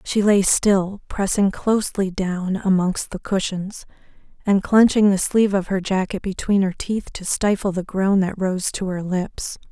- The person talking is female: Yes, female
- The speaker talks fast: No, average, 175 wpm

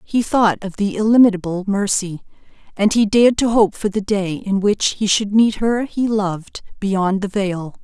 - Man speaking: No, female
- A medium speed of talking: Yes, average, 190 wpm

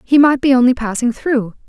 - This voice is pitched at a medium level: No, very high, 250 Hz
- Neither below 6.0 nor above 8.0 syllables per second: No, 5.4 syllables/s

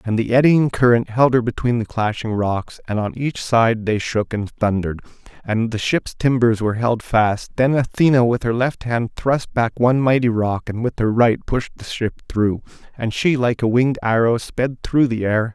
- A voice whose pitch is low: Yes, low, 115 Hz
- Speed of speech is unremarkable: No, fast, 210 wpm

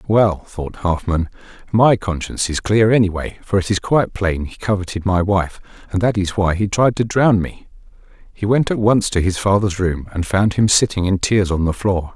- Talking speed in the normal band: No, fast, 210 wpm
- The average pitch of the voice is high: No, low, 100 Hz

